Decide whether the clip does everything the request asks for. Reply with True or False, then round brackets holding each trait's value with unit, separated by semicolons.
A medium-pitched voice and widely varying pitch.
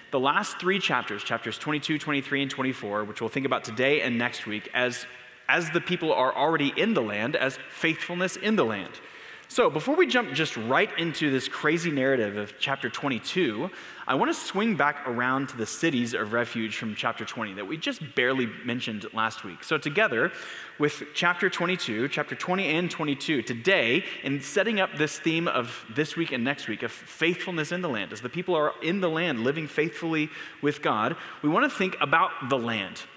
True (145 Hz; 6.0 semitones)